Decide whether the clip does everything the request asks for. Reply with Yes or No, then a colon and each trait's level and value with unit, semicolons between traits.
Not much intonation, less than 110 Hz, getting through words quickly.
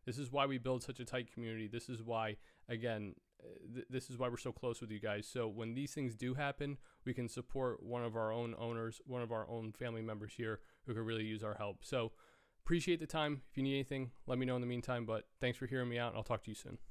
No: narrow, 2.3 semitones; low, 120 Hz; fast, 270 wpm